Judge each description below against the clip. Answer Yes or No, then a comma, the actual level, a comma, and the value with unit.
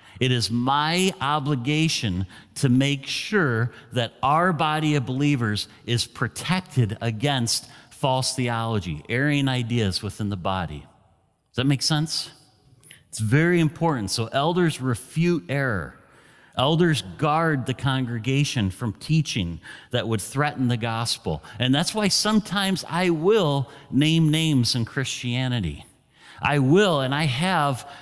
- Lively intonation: No, average, 4.6 semitones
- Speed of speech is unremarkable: No, slow, 125 wpm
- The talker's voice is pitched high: No, low, 135 Hz